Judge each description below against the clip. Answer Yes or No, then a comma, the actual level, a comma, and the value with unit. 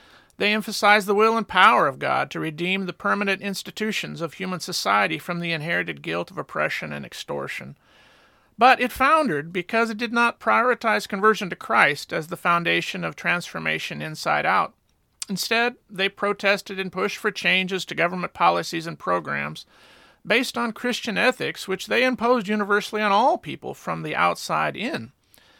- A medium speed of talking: Yes, average, 160 wpm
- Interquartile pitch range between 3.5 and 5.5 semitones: Yes, average, 4.2 semitones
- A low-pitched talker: No, high, 205 Hz